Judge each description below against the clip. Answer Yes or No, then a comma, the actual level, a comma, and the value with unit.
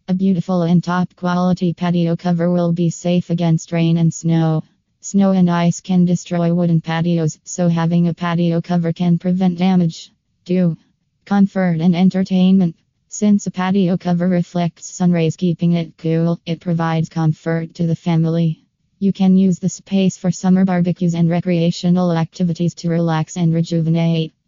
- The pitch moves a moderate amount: No, narrow, 1.5 semitones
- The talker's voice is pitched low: No, medium, 175 Hz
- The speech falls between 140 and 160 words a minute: Yes, average, 155 wpm